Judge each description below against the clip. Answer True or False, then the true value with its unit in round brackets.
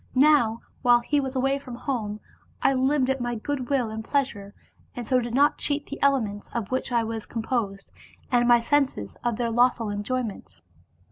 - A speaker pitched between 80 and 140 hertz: False (245 Hz)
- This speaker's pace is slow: False (185 wpm)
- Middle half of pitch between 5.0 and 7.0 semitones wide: False (3.2 semitones)